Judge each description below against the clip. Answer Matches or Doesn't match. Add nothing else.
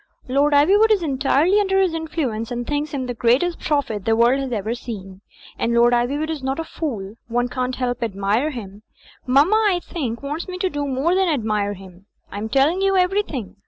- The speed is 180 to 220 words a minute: Matches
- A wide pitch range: Matches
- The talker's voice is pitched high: Matches